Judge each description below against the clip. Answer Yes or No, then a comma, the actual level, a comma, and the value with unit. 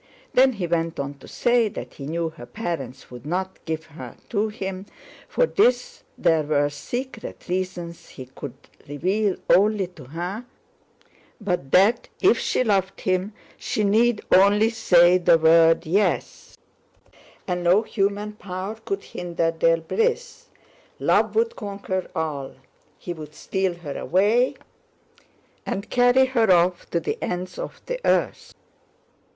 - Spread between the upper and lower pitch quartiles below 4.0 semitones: No, average, 4.4 semitones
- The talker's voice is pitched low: No, medium, 185 Hz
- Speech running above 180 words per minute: No, slow, 135 wpm